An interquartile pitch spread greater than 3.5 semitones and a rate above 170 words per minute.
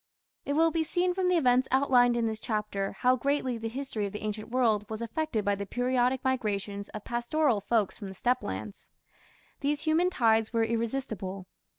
Yes: average, 4.1 semitones; average, 190 wpm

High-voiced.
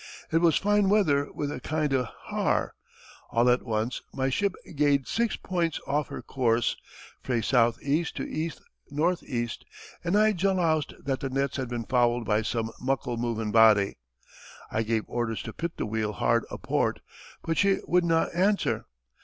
No: low, 135 Hz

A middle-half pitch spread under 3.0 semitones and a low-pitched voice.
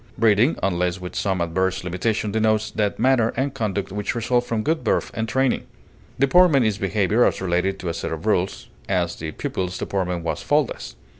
No: average, 4.2 semitones; low, 105 Hz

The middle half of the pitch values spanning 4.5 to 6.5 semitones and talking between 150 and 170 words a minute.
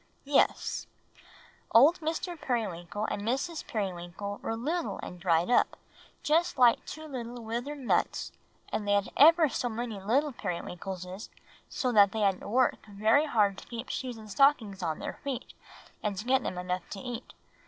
Yes: wide, 5.4 semitones; average, 165 wpm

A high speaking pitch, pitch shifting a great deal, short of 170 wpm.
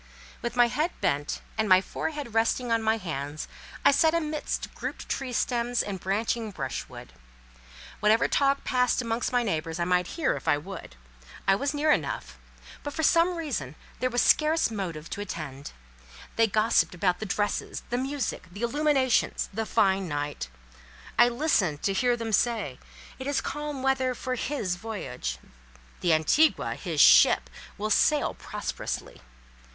Yes: high, 225 Hz; wide, 6.3 semitones; average, 155 wpm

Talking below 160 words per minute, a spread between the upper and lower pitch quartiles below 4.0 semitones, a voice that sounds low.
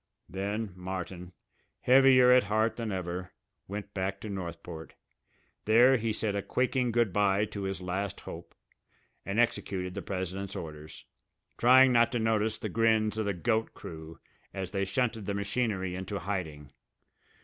Yes: average, 150 wpm; average, 3.5 semitones; low, 100 Hz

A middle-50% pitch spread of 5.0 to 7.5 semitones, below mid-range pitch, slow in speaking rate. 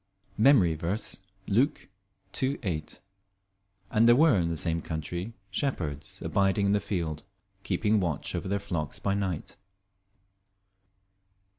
No: average, 4.6 semitones; very low, 95 Hz; slow, 125 wpm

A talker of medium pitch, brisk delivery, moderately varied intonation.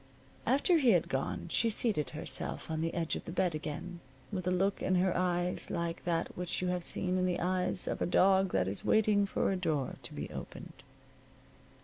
No: medium, 180 Hz; fast, 210 wpm; narrow, 2.2 semitones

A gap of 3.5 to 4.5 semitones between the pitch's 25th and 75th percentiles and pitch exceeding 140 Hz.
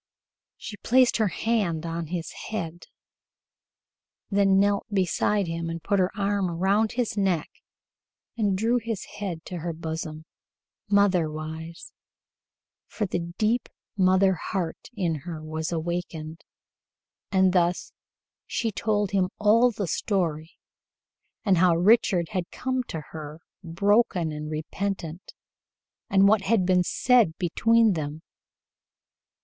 Yes: average, 3.8 semitones; medium, 185 Hz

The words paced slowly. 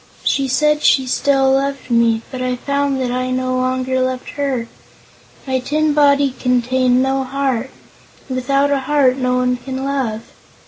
No: average, 165 wpm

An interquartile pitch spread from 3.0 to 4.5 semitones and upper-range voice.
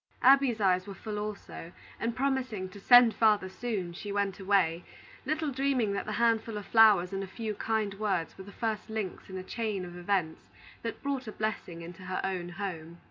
Yes: average, 3.4 semitones; high, 205 Hz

